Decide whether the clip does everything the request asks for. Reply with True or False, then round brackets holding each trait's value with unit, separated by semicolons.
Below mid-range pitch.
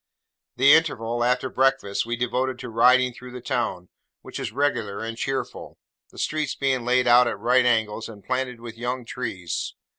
True (125 Hz)